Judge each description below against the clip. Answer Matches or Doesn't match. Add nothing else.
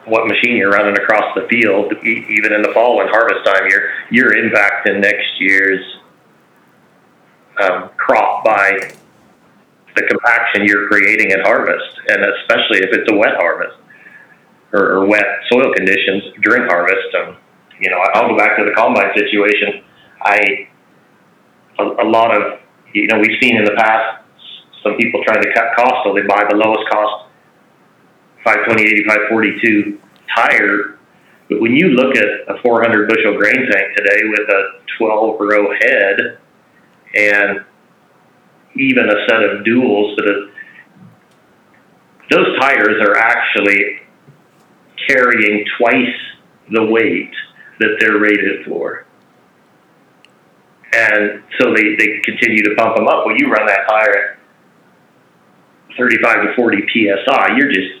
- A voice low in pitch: Matches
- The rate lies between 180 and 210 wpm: Doesn't match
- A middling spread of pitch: Doesn't match